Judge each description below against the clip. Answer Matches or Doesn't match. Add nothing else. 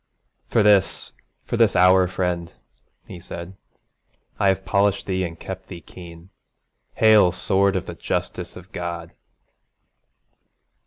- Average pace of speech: Doesn't match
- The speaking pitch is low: Matches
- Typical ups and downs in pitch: Doesn't match